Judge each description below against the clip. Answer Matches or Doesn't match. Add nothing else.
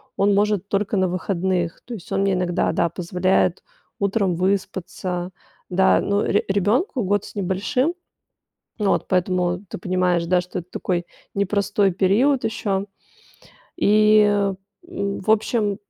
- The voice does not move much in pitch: Matches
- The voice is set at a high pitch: Matches